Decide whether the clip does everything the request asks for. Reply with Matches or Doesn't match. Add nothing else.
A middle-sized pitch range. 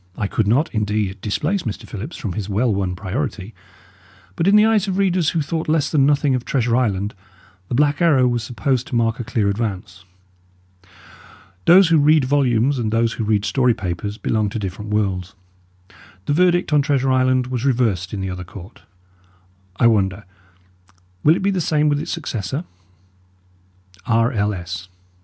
Doesn't match